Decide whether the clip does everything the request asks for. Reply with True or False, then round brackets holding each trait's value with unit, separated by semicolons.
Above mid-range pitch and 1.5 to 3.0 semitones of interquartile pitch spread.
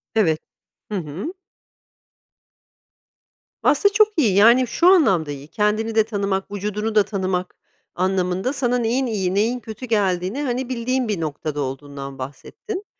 False (210 Hz; 5.3 semitones)